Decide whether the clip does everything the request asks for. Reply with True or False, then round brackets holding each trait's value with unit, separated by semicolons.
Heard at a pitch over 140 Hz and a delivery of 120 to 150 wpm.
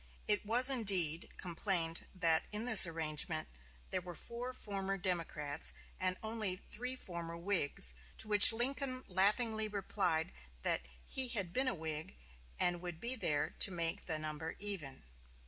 True (185 Hz; 145 wpm)